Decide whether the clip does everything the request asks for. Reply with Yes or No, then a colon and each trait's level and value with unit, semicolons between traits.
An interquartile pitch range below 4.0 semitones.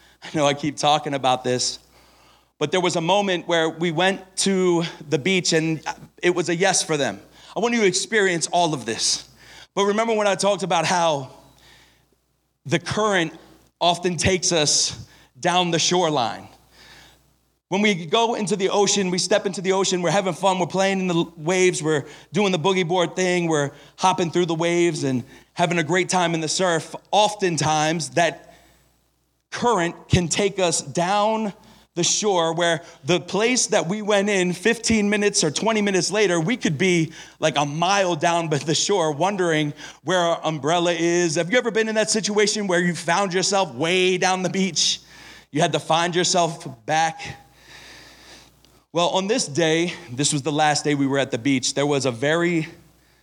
Yes: average, 3.3 semitones